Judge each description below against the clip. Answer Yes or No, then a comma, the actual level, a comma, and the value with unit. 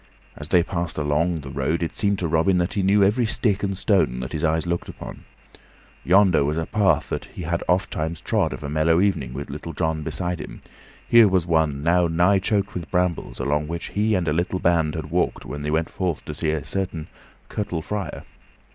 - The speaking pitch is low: Yes, very low, 85 Hz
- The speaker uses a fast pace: Yes, fast, 215 wpm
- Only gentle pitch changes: No, average, 3.4 semitones